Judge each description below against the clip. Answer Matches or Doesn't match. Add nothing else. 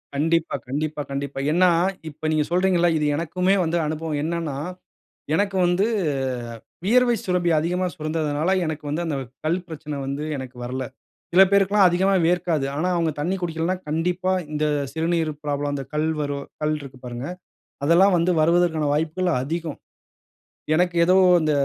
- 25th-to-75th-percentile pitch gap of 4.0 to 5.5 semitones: Doesn't match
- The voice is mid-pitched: Matches